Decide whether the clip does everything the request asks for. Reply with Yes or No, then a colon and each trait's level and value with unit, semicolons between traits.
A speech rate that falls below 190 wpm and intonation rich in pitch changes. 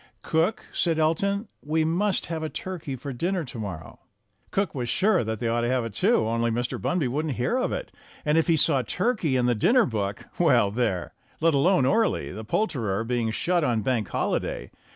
No: average, 200 wpm; wide, 7.3 semitones